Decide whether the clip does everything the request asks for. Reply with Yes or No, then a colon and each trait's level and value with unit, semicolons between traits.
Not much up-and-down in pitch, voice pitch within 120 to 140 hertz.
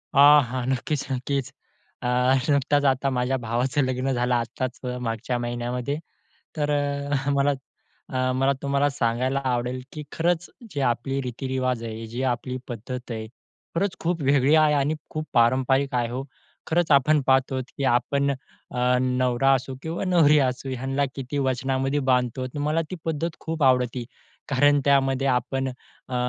Yes: narrow, 2.2 semitones; low, 135 Hz